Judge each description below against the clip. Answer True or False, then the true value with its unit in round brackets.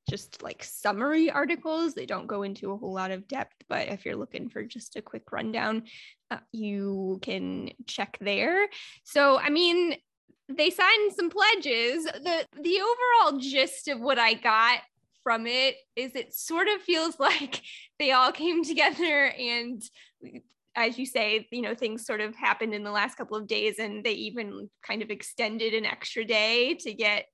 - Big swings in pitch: True (6.3 semitones)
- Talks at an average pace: True (180 wpm)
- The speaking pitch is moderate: False (250 Hz)